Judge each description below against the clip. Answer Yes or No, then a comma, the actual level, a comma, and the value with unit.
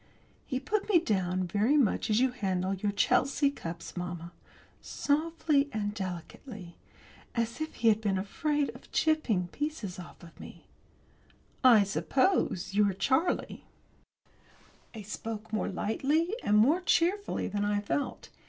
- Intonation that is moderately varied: No, wide, 6.9 semitones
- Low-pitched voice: No, high, 220 Hz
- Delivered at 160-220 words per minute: No, slow, 135 wpm